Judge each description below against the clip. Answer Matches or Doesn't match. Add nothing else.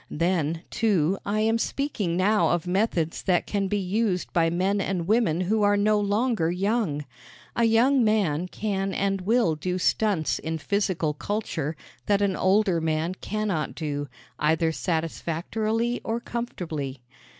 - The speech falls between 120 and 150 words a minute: Matches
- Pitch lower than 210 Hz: Matches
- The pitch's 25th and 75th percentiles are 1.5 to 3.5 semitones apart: Doesn't match